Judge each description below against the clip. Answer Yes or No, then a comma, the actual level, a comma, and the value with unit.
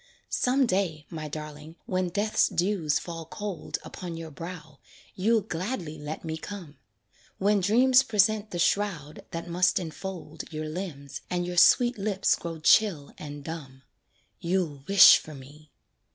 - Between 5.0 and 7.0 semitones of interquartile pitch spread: No, average, 4.5 semitones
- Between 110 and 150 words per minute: Yes, average, 145 wpm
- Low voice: No, medium, 175 Hz